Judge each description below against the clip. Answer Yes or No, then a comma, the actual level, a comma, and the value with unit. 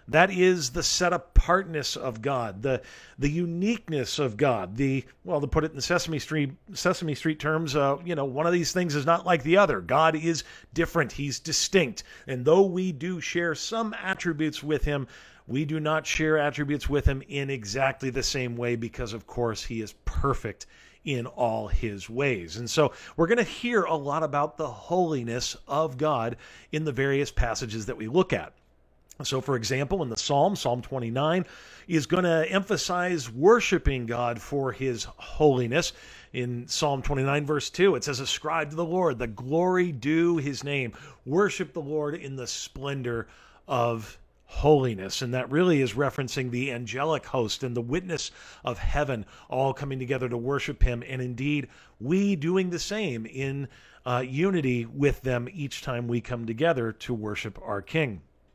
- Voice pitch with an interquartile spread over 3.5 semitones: Yes, average, 4.8 semitones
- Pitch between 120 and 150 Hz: Yes, medium, 140 Hz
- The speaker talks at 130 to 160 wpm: No, average, 175 wpm